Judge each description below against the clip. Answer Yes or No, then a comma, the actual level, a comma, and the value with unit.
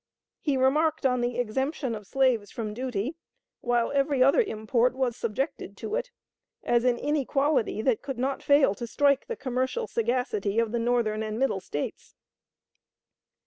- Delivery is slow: No, average, 155 wpm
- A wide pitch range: No, average, 3.2 semitones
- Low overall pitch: No, very high, 250 Hz